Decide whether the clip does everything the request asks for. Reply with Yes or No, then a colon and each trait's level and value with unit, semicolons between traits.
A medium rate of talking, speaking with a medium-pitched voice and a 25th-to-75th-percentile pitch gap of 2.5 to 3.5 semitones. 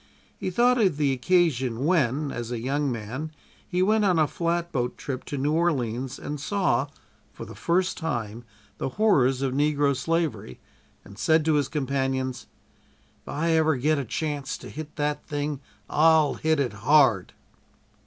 No: average, 160 wpm; medium, 145 Hz; average, 3.9 semitones